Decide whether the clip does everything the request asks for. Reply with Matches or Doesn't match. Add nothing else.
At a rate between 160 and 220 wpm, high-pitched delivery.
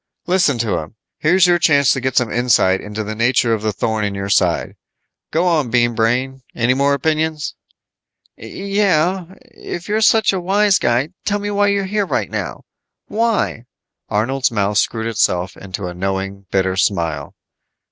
Doesn't match